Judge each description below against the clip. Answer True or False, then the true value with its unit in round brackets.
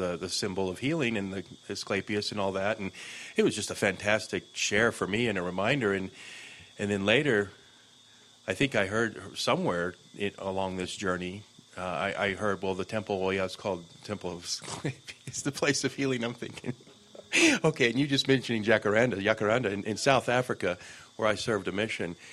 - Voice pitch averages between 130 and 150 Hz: False (105 Hz)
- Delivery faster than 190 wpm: True (200 wpm)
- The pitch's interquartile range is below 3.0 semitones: False (4.5 semitones)